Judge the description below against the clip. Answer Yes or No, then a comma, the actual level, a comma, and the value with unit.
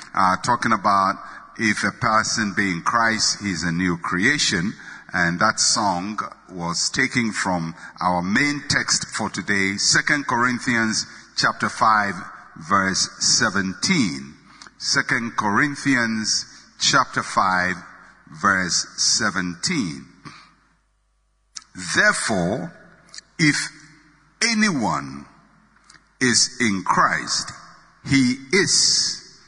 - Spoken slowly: Yes, slow, 90 wpm